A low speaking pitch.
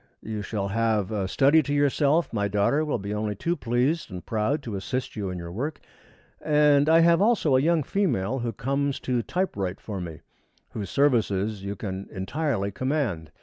Yes: low, 115 Hz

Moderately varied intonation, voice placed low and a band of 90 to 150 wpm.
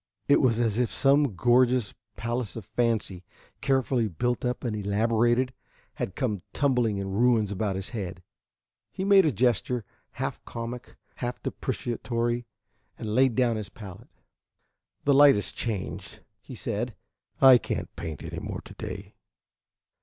Yes: average, 3.1 semitones; low, 120 Hz; average, 145 wpm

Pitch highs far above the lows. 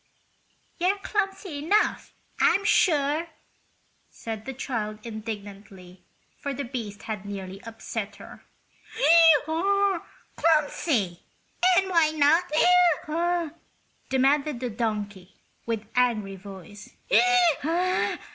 Yes: wide, 8.0 semitones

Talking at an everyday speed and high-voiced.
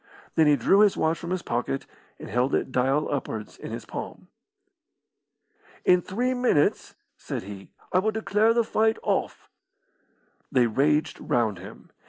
No: average, 155 wpm; medium, 150 Hz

